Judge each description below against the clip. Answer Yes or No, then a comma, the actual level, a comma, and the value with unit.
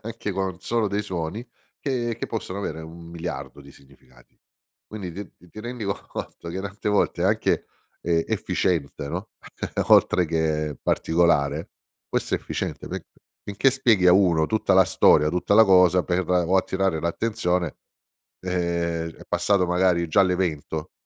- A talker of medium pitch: No, very low, 90 Hz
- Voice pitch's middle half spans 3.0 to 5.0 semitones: Yes, average, 3.4 semitones